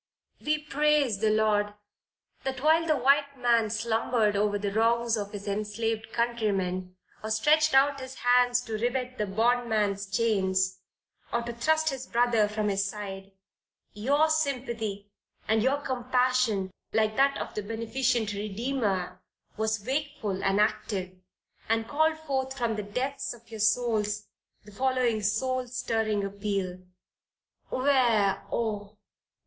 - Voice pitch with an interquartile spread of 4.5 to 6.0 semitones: No, average, 3.8 semitones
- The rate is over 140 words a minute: No, slow, 135 wpm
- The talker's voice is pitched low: No, high, 225 Hz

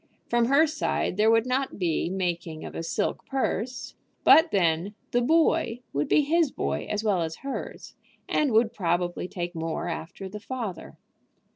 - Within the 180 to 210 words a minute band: No, average, 165 wpm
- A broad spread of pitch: Yes, wide, 6.8 semitones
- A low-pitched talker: No, high, 210 Hz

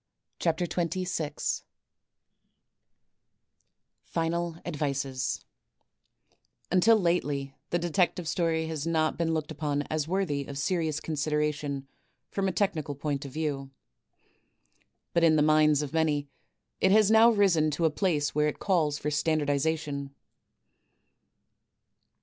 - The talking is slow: Yes, slow, 115 wpm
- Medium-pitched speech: Yes, medium, 155 Hz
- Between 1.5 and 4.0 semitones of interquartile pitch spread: Yes, average, 2.7 semitones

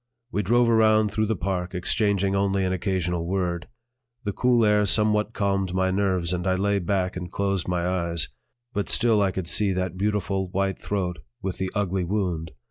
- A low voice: Yes, very low, 95 Hz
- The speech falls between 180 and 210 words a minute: Yes, average, 185 wpm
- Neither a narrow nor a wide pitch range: No, narrow, 2.2 semitones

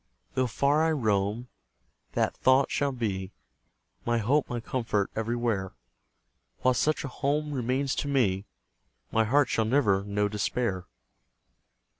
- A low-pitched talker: Yes, low, 120 Hz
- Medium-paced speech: No, slow, 130 wpm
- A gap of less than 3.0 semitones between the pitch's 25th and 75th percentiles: No, average, 5.0 semitones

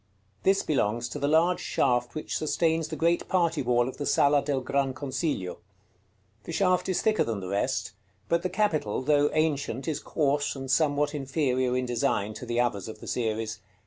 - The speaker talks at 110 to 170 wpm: No, average, 185 wpm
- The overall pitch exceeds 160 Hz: No, medium, 140 Hz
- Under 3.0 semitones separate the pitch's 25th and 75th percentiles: No, average, 4.6 semitones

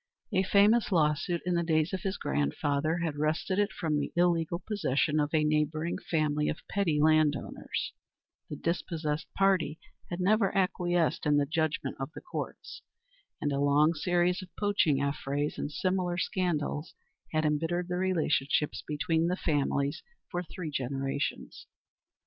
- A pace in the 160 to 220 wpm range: No, average, 150 wpm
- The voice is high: No, medium, 160 Hz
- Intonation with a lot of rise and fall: No, average, 3.2 semitones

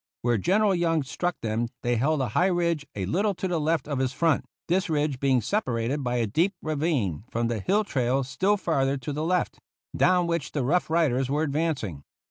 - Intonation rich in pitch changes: Yes, wide, 5.7 semitones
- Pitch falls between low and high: Yes, medium, 150 Hz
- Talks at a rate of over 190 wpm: Yes, fast, 205 wpm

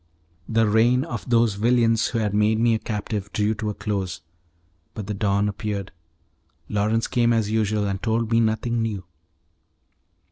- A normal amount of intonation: No, narrow, 1.8 semitones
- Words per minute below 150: No, average, 165 wpm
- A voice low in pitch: Yes, low, 110 Hz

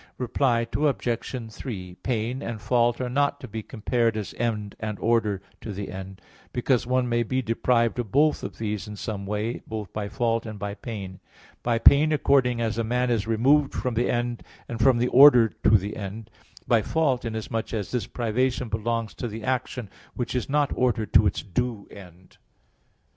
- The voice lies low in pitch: Yes, low, 115 Hz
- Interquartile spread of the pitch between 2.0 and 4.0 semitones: Yes, average, 2.7 semitones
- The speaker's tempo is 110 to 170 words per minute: No, average, 185 wpm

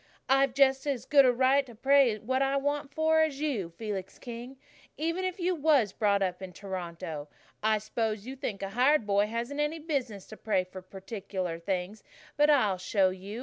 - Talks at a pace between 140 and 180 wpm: No, average, 190 wpm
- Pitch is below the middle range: No, high, 230 Hz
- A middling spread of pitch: No, wide, 6.0 semitones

